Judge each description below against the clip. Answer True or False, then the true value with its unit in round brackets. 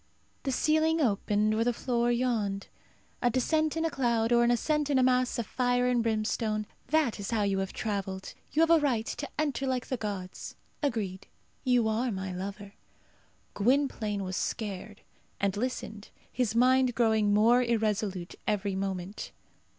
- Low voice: False (230 Hz)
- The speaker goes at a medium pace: True (165 wpm)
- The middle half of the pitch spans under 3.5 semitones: False (3.8 semitones)